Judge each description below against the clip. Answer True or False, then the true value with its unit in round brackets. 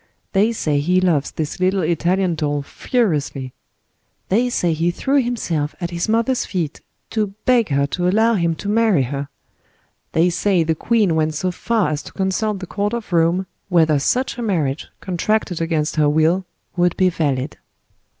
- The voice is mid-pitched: True (175 Hz)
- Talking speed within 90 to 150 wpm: False (170 wpm)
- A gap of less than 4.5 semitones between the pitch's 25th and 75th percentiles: False (4.8 semitones)